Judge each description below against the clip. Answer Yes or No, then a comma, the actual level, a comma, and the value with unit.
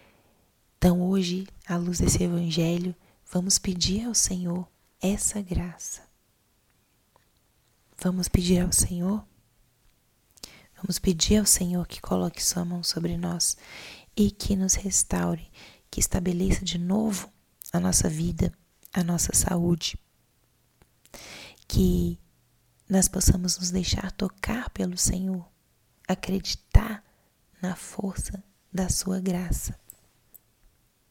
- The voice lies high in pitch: No, medium, 180 Hz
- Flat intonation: Yes, narrow, 2.2 semitones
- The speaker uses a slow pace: Yes, slow, 105 wpm